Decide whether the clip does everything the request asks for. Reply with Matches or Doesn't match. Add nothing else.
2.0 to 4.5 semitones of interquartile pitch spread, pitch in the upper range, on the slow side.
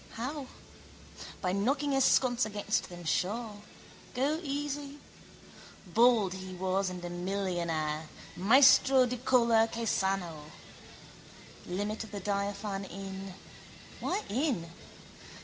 Doesn't match